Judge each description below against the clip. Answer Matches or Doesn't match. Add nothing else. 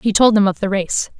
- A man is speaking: Doesn't match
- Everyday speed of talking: Doesn't match